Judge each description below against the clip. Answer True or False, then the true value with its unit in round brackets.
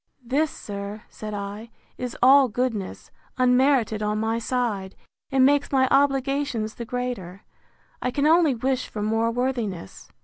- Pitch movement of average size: True (3.8 semitones)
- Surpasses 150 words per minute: False (140 wpm)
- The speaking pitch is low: False (245 Hz)